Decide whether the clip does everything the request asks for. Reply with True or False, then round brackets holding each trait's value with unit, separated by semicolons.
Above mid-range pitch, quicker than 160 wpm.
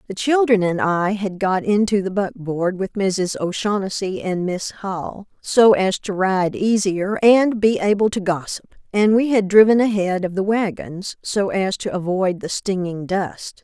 True (195 Hz; 175 wpm)